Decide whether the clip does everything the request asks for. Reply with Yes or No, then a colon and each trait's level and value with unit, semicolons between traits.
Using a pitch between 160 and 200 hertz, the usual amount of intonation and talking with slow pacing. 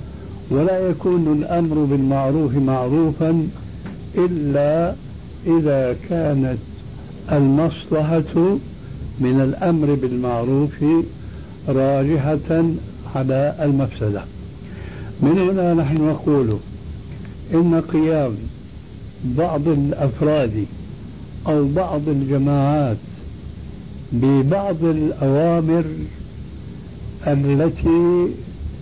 No: medium, 145 Hz; average, 3.5 semitones; slow, 60 wpm